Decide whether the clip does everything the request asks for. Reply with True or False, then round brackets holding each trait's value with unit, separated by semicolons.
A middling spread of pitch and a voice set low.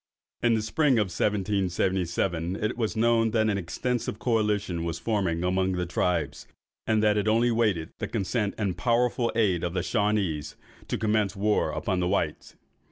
True (3.6 semitones; 105 Hz)